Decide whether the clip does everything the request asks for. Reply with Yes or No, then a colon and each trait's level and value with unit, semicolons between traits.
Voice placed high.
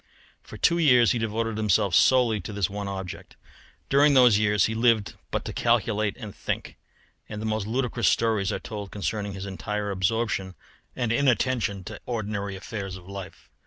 No: low, 105 Hz